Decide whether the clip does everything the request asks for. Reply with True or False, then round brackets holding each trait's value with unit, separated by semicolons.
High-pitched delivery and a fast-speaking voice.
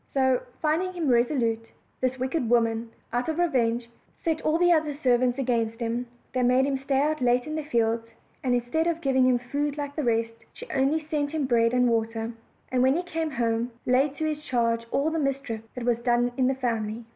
True (255 Hz; 215 wpm)